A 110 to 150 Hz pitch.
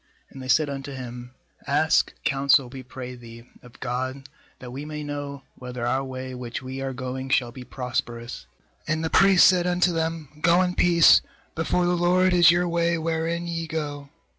Yes: medium, 140 Hz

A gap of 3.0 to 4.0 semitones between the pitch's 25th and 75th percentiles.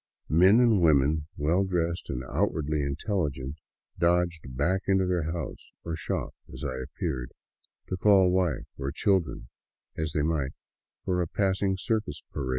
No: average, 4.6 semitones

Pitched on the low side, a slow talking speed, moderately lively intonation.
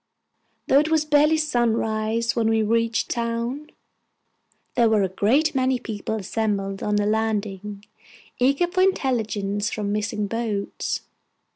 No: high, 225 Hz; slow, 130 wpm; average, 3.7 semitones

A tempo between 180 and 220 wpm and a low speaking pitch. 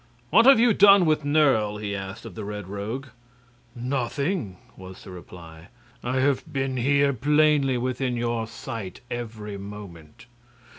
No: average, 145 wpm; low, 120 Hz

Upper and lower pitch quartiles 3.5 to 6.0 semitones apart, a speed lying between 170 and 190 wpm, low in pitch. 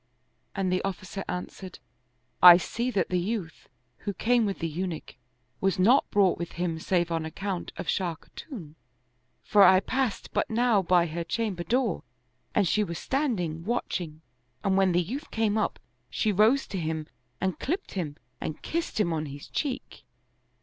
No: average, 4.4 semitones; average, 175 wpm; high, 190 Hz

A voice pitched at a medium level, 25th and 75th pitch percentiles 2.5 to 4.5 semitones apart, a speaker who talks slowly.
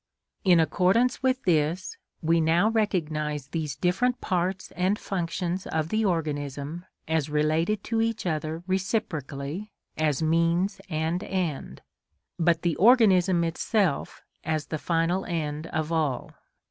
Yes: medium, 170 Hz; average, 3.4 semitones; slow, 125 wpm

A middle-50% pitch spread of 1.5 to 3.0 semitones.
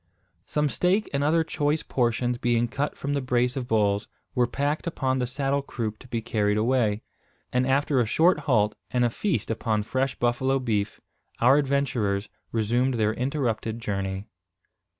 No: average, 3.8 semitones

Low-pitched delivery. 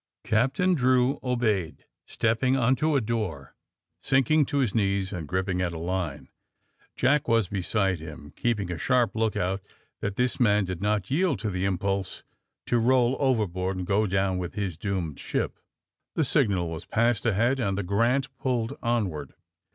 Yes: low, 105 Hz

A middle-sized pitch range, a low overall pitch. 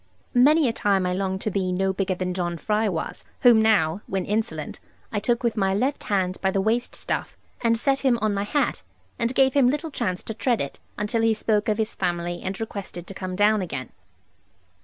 No: average, 3.6 semitones; high, 205 Hz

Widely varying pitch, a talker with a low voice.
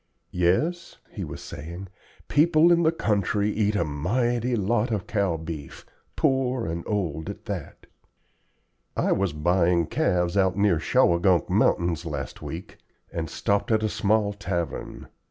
No: average, 4.4 semitones; very low, 95 Hz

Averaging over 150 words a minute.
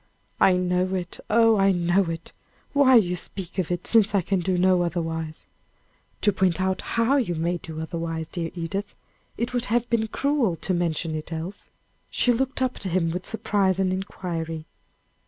Yes: average, 185 wpm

